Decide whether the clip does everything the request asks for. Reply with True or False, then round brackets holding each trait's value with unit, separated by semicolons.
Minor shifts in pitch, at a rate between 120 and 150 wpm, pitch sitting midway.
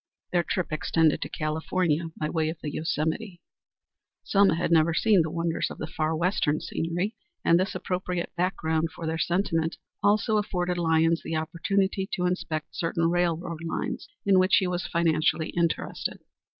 False (2.2 semitones; 160 wpm; 170 Hz)